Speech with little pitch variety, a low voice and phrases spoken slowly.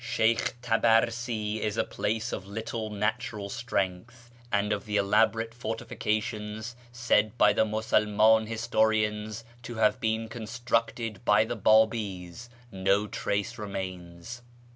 Yes: narrow, 1.7 semitones; low, 110 Hz; slow, 120 wpm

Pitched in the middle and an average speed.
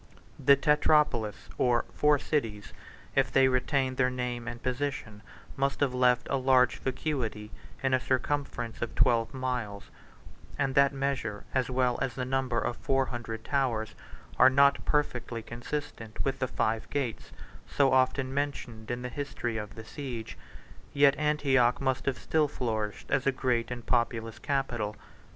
No: low, 130 Hz; average, 155 wpm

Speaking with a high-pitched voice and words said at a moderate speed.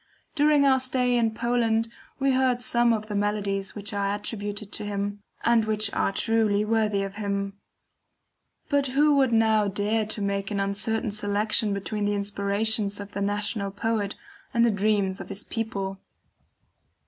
Yes: high, 210 Hz; average, 160 wpm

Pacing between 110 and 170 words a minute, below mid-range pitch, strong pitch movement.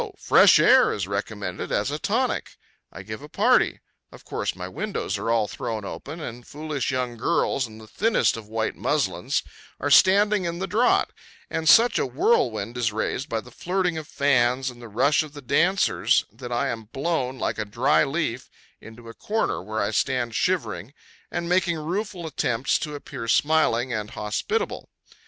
No: average, 180 wpm; low, 130 Hz; wide, 6.9 semitones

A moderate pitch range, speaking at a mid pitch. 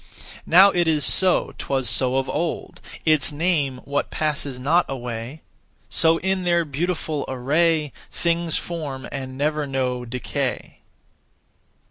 Yes: average, 4.1 semitones; medium, 150 Hz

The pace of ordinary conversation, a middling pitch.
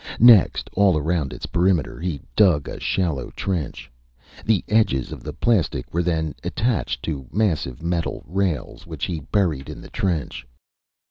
No: average, 150 wpm; very low, 85 Hz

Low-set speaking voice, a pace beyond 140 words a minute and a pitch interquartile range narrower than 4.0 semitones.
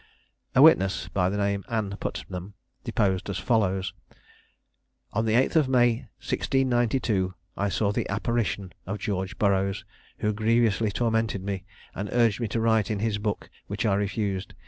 Yes: low, 105 Hz; average, 150 wpm; average, 2.7 semitones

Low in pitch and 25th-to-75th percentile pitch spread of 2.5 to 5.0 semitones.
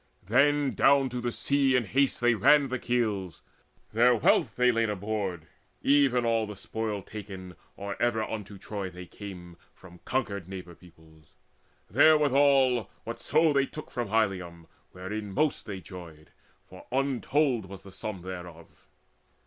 No: low, 110 Hz; wide, 5.6 semitones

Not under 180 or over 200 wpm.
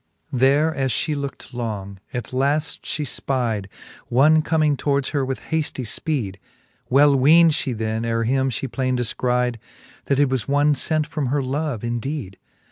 No: average, 165 wpm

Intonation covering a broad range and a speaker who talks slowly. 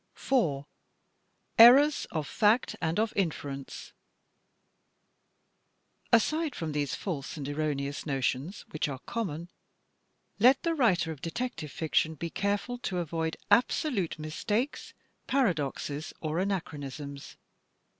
Yes: wide, 7.6 semitones; slow, 105 wpm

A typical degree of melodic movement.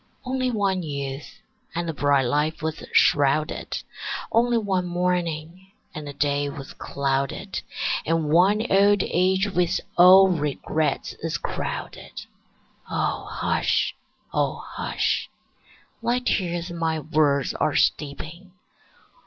Yes: average, 4.3 semitones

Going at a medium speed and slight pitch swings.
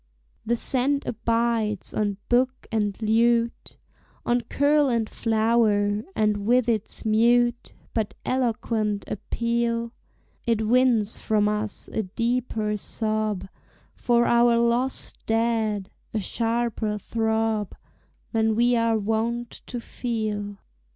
No: slow, 110 wpm; narrow, 1.8 semitones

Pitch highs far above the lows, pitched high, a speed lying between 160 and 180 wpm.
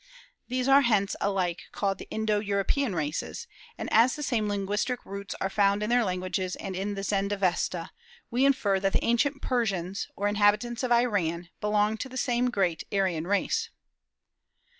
No: average, 3.7 semitones; high, 205 Hz; average, 170 wpm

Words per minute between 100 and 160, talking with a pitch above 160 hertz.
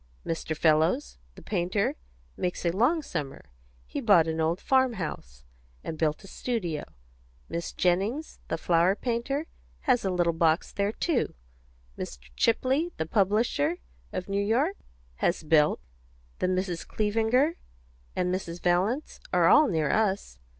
Yes: average, 140 wpm; medium, 185 Hz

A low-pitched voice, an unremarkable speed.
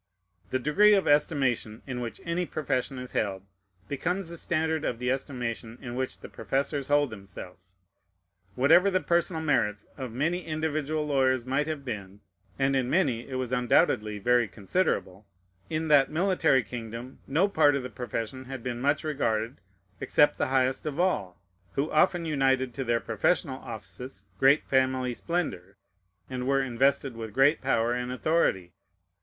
Yes: low, 130 Hz; average, 160 wpm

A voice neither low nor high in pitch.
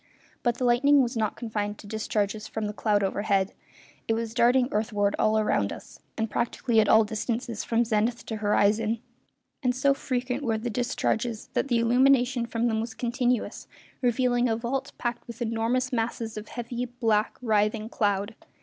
No: high, 230 Hz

